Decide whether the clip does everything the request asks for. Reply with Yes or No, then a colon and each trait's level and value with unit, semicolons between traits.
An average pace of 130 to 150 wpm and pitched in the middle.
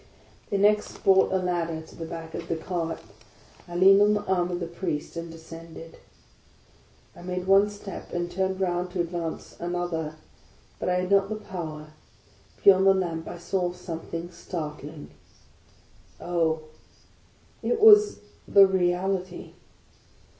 Yes: average, 145 wpm; medium, 175 Hz